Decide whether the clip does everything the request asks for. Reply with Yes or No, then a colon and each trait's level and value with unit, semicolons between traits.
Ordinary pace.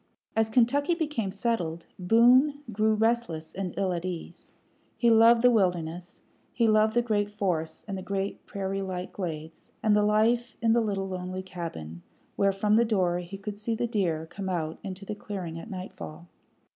Yes: average, 180 wpm